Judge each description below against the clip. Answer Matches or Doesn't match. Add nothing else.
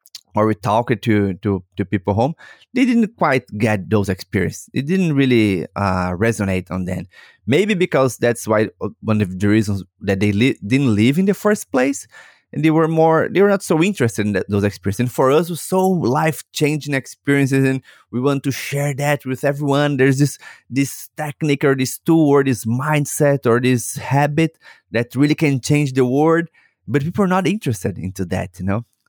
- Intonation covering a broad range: Matches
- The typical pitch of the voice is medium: Doesn't match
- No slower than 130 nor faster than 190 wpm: Doesn't match